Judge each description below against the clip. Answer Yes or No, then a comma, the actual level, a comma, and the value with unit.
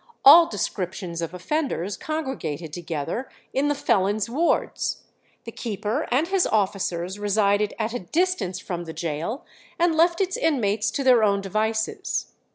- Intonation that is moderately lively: No, wide, 7.6 semitones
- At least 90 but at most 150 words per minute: Yes, average, 145 wpm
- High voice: Yes, high, 215 Hz